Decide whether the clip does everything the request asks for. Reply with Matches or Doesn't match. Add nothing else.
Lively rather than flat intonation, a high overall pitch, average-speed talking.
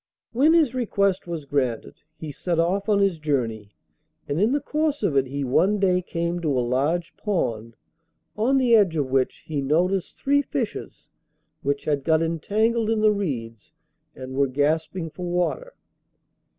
Doesn't match